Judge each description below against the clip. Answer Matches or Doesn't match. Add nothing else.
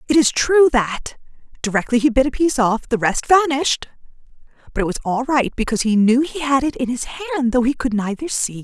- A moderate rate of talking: Doesn't match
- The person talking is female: Matches